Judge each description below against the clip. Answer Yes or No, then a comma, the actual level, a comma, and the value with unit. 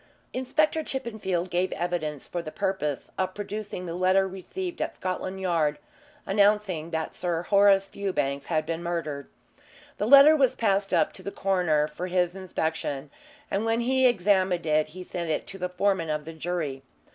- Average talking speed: Yes, average, 170 wpm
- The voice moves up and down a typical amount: Yes, average, 3.6 semitones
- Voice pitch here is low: No, medium, 185 Hz